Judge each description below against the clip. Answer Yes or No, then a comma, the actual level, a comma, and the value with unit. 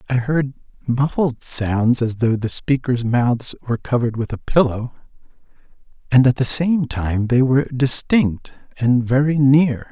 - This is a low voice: Yes, low, 125 Hz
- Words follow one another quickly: No, average, 150 wpm